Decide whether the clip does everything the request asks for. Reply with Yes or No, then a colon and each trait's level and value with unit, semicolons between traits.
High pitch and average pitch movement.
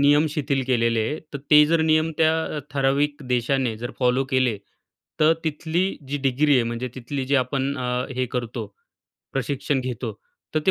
No: low, 135 Hz; average, 3.0 semitones